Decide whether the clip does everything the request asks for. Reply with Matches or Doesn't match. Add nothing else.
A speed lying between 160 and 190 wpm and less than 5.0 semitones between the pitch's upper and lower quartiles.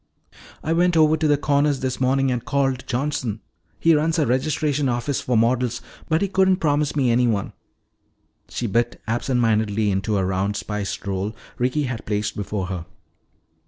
Doesn't match